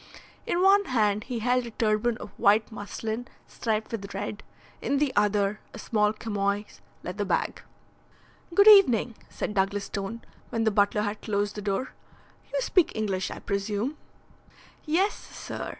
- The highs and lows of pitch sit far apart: No, average, 3.2 semitones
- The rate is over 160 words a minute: No, average, 150 wpm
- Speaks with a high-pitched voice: Yes, high, 215 Hz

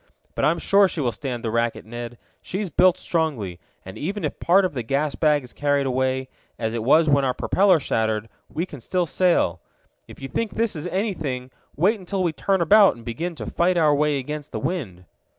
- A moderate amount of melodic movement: No, wide, 6.3 semitones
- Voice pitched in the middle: Yes, medium, 150 Hz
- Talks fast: Yes, fast, 210 wpm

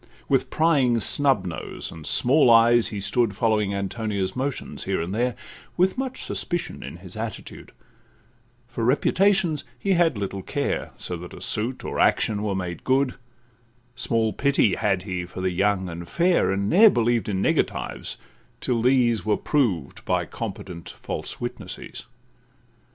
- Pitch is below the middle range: Yes, low, 115 Hz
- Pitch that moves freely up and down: Yes, wide, 5.7 semitones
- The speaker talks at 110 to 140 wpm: No, average, 150 wpm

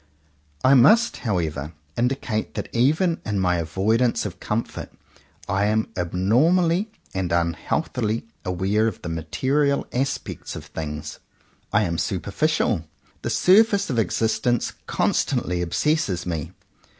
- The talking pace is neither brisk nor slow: No, slow, 115 wpm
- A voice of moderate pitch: No, low, 110 Hz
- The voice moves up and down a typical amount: No, wide, 7.6 semitones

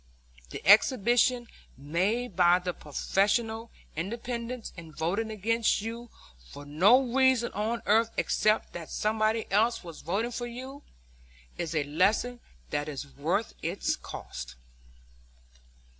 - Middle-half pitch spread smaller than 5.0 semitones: No, wide, 5.6 semitones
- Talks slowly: Yes, slow, 120 wpm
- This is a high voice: Yes, high, 215 Hz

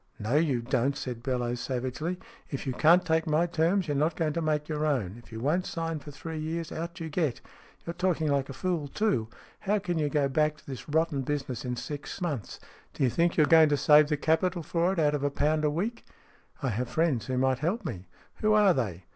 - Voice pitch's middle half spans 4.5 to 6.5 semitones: No, average, 3.9 semitones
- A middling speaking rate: No, fast, 245 wpm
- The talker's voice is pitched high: No, medium, 150 Hz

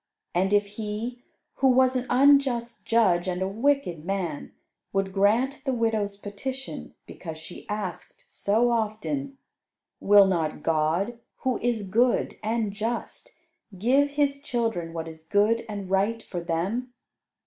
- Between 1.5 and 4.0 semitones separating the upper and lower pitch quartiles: No, average, 4.4 semitones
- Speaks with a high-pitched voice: Yes, high, 215 Hz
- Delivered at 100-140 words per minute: Yes, slow, 135 wpm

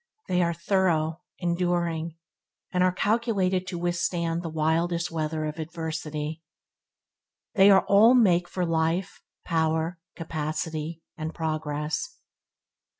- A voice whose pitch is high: No, medium, 170 Hz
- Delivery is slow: Yes, slow, 105 wpm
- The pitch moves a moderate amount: No, narrow, 2.2 semitones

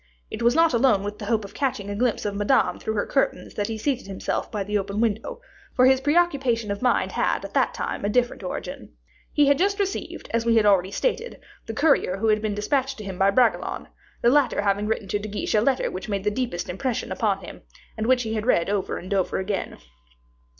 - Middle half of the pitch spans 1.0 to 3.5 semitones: No, average, 4.2 semitones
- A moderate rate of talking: No, fast, 235 wpm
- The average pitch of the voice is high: Yes, high, 220 Hz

